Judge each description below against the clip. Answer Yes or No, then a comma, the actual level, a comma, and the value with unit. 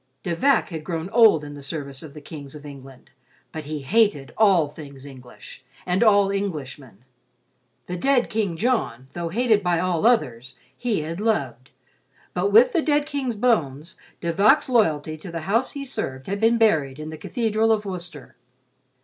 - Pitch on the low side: No, medium, 175 Hz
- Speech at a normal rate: Yes, average, 175 wpm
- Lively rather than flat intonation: Yes, wide, 7.3 semitones